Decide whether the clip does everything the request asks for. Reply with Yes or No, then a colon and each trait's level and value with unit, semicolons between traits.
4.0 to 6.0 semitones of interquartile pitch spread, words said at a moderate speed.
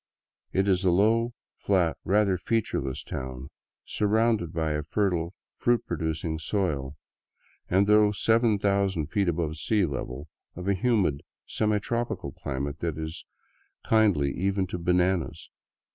No: average, 4.7 semitones; slow, 130 wpm